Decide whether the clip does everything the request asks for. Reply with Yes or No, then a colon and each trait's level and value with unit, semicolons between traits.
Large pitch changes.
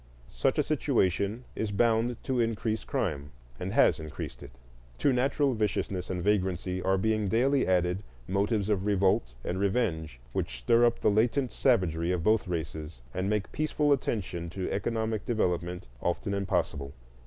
No: average, 4.3 semitones